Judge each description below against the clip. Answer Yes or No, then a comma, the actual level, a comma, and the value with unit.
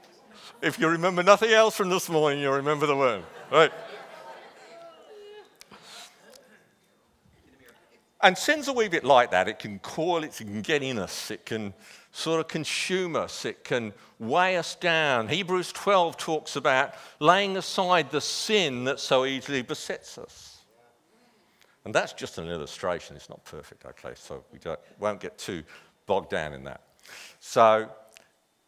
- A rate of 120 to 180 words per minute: Yes, average, 155 wpm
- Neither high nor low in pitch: Yes, medium, 160 Hz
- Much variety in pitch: Yes, wide, 6.3 semitones